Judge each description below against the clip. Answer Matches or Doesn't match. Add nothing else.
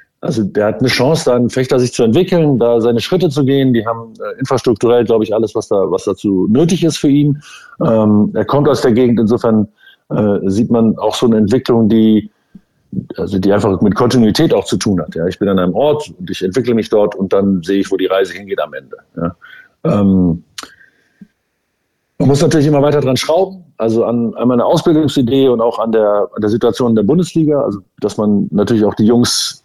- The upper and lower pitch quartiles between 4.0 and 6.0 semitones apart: Matches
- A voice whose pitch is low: Matches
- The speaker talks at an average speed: Doesn't match